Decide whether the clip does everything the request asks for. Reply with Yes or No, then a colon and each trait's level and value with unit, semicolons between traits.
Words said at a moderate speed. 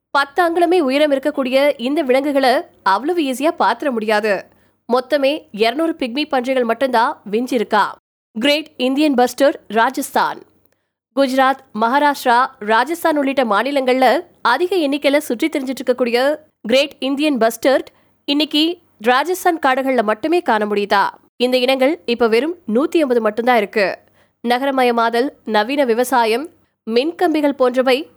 Yes: average, 110 wpm